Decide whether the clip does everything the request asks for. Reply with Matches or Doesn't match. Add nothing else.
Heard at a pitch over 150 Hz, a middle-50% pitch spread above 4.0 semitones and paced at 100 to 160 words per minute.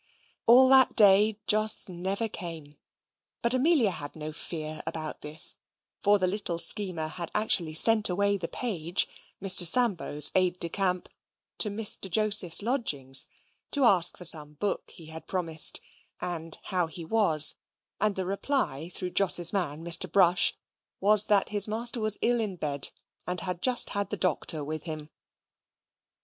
Matches